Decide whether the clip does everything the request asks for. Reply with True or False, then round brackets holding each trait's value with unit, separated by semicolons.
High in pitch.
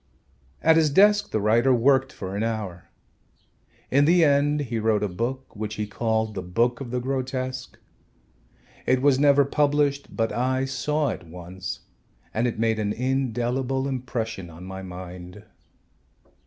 False (120 Hz)